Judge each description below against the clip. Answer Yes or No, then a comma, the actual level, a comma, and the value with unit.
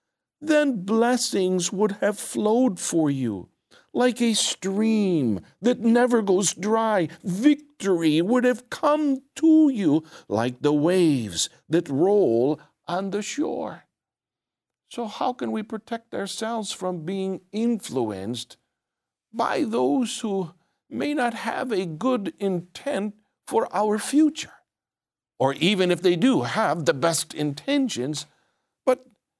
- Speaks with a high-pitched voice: Yes, high, 205 Hz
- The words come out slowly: Yes, slow, 120 wpm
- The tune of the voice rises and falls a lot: Yes, wide, 6.2 semitones